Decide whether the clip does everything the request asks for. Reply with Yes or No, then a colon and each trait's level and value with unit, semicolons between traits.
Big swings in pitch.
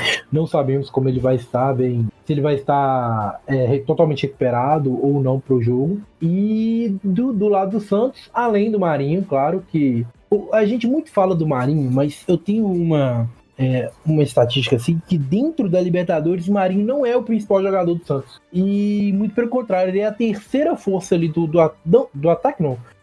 Yes: wide, 7.0 semitones